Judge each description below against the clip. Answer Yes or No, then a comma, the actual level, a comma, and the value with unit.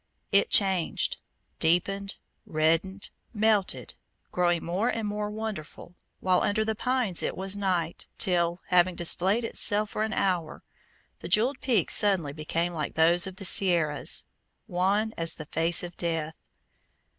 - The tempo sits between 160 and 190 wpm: No, average, 140 wpm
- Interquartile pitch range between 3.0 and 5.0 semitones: Yes, average, 3.6 semitones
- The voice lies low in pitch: No, medium, 185 Hz